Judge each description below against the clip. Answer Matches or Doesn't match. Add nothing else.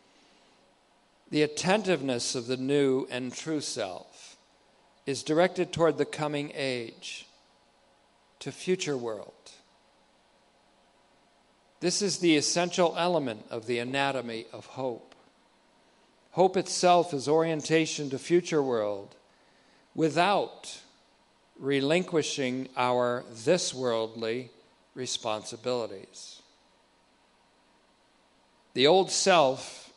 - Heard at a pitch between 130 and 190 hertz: Matches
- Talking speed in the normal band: Doesn't match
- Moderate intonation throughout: Matches